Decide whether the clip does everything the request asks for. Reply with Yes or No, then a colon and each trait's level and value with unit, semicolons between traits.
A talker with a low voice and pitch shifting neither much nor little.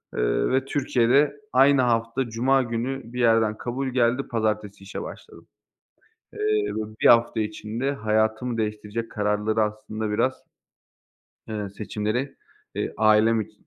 Yes: low, 115 Hz; average, 3.1 semitones